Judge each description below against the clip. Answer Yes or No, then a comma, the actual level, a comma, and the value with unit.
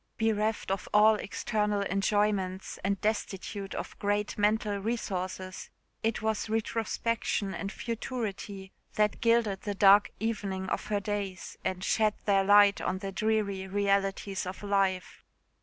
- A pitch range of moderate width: No, narrow, 1.8 semitones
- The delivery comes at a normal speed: No, slow, 130 wpm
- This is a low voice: No, high, 205 Hz